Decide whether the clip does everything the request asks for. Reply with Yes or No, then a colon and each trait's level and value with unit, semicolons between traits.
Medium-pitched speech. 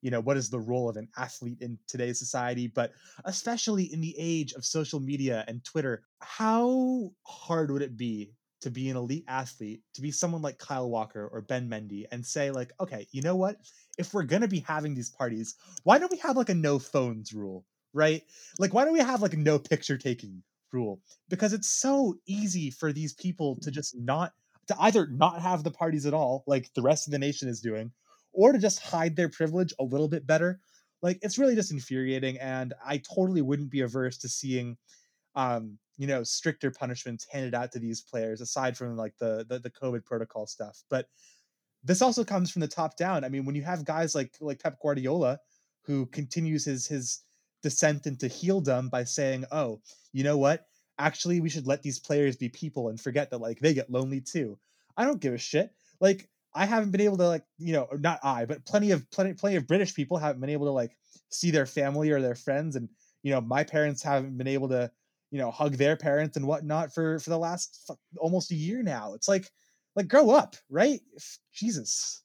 Yes: medium, 145 Hz